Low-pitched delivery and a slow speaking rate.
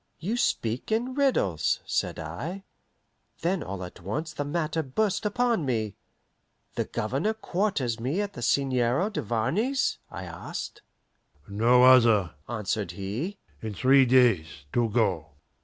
Yes: low, 130 Hz; slow, 130 wpm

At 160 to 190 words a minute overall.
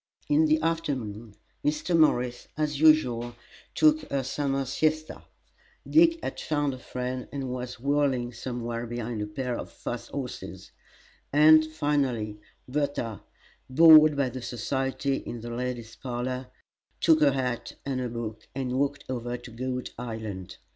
No: average, 140 wpm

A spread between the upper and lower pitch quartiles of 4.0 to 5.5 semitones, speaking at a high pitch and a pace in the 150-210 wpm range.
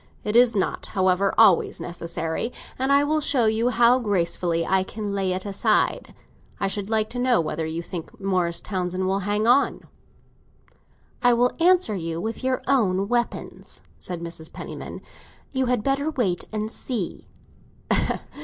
Yes: average, 5.1 semitones; high, 205 Hz; average, 155 wpm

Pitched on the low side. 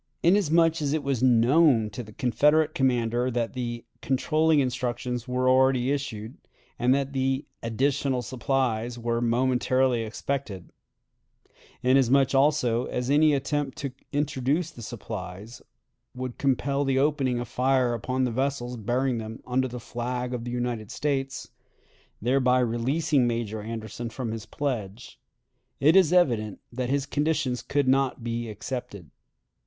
Yes: low, 125 Hz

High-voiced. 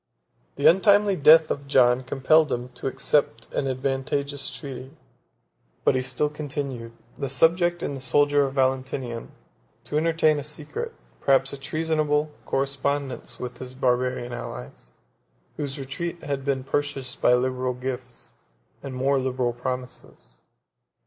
No: low, 135 Hz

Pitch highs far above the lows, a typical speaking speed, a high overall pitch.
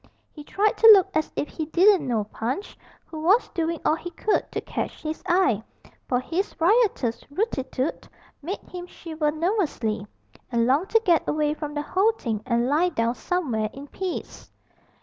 Yes: wide, 6.0 semitones; average, 170 wpm; very high, 315 Hz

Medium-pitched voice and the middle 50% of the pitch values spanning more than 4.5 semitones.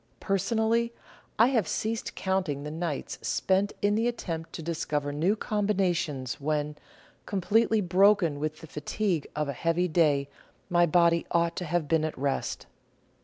Yes: medium, 170 Hz; average, 5.0 semitones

